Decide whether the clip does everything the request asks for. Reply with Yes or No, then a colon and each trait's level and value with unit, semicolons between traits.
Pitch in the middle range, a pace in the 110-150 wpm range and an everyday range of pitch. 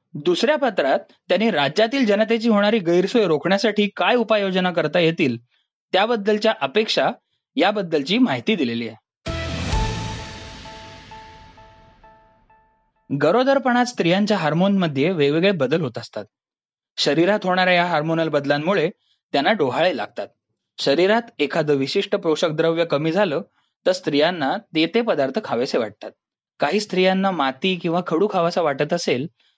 No: medium, 180 Hz; average, 115 wpm; wide, 6.5 semitones